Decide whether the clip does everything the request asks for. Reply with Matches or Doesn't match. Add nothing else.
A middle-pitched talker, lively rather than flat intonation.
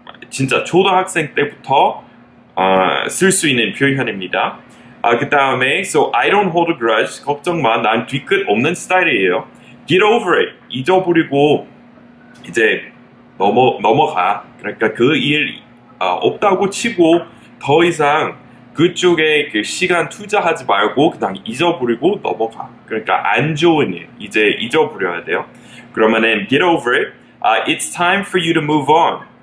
Matches